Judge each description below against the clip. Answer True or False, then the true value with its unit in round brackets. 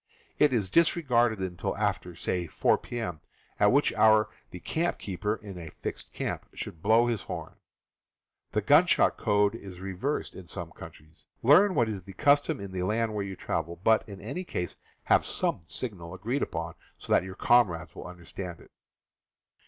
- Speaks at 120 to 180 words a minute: True (170 wpm)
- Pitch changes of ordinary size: True (5.0 semitones)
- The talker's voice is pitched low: True (100 Hz)